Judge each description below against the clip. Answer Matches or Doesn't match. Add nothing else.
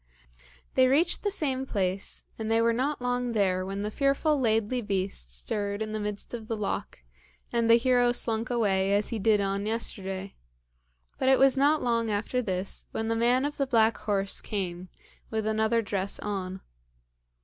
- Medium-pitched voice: Doesn't match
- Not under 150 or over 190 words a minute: Matches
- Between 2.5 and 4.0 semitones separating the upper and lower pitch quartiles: Matches